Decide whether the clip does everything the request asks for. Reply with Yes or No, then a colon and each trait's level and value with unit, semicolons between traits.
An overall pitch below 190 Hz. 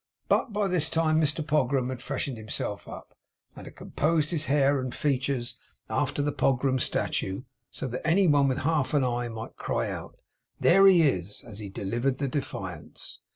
Yes: medium, 140 Hz